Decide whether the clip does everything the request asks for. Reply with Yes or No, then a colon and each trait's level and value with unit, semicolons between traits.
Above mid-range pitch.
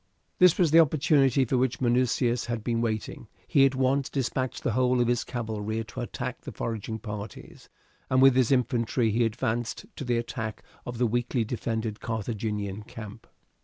No: low, 120 Hz